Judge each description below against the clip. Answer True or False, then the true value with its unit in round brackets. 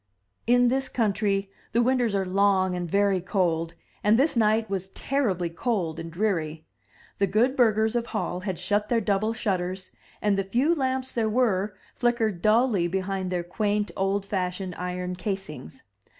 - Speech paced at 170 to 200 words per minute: False (160 wpm)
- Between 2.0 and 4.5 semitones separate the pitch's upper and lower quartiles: True (3.6 semitones)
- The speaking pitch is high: True (200 Hz)